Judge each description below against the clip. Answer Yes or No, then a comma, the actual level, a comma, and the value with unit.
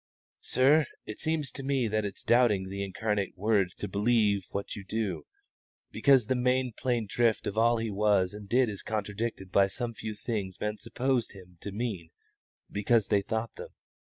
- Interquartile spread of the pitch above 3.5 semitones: No, average, 3.2 semitones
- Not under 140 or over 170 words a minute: No, average, 180 wpm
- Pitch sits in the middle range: No, low, 110 Hz